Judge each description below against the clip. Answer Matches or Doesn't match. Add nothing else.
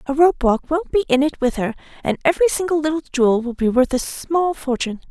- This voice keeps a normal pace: Doesn't match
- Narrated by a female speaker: Matches